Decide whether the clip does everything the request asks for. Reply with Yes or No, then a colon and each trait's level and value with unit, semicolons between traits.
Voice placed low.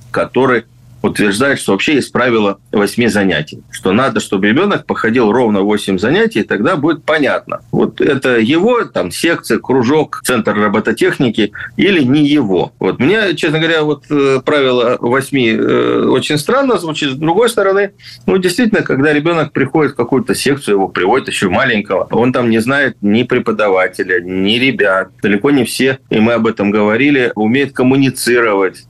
Yes: low, 125 Hz